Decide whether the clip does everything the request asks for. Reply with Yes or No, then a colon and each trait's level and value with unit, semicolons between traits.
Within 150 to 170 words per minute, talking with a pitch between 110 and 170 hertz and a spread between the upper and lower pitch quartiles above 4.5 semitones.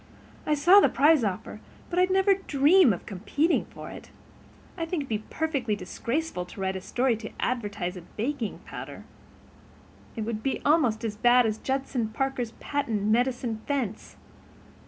No: average, 165 wpm; high, 245 Hz; average, 5.2 semitones